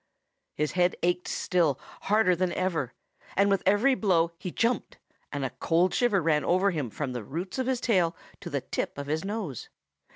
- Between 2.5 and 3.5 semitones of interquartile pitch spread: No, average, 4.4 semitones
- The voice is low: No, medium, 180 Hz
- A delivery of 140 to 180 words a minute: No, average, 190 wpm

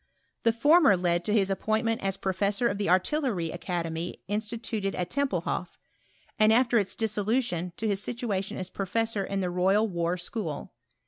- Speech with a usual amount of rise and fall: Yes, average, 3.7 semitones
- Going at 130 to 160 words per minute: No, average, 170 wpm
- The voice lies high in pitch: Yes, high, 200 Hz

